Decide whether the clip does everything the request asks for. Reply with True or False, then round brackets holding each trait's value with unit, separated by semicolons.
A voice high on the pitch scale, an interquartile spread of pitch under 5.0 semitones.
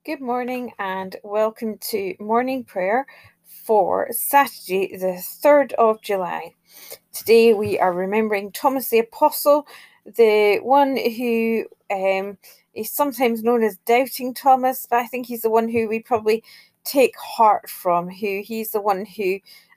True (225 Hz; 3.7 semitones)